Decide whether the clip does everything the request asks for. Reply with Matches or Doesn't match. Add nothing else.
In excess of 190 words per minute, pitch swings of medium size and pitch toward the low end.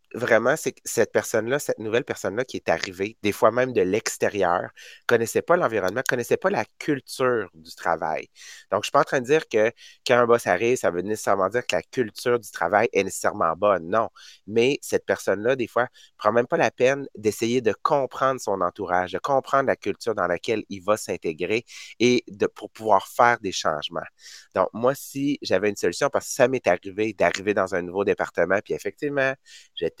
Matches